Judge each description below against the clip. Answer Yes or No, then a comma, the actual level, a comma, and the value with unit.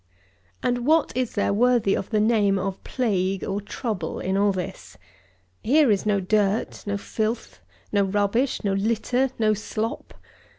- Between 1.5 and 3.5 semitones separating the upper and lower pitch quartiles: Yes, average, 3.2 semitones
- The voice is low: No, high, 210 Hz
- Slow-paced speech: No, average, 160 wpm